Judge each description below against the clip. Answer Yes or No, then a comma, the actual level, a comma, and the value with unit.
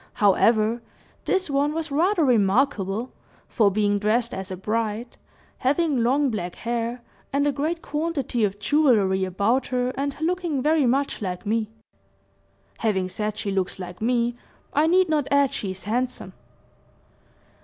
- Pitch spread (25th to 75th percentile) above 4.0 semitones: Yes, wide, 5.4 semitones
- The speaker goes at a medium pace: Yes, average, 145 wpm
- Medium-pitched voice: No, high, 240 Hz